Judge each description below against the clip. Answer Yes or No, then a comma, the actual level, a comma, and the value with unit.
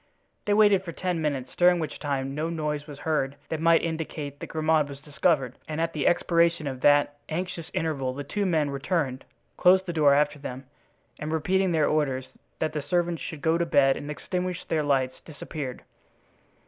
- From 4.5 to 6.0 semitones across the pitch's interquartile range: No, average, 2.8 semitones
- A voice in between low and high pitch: Yes, medium, 155 Hz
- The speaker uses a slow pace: No, average, 185 wpm